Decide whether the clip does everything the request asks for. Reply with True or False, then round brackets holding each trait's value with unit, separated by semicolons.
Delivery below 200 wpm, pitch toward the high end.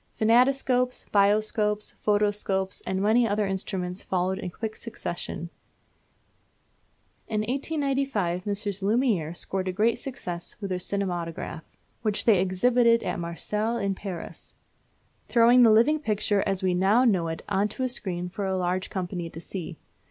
True (145 wpm; 200 Hz)